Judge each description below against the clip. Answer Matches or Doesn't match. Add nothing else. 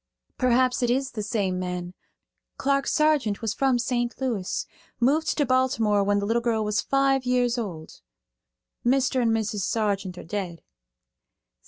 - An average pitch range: Matches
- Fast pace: Doesn't match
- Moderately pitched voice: Doesn't match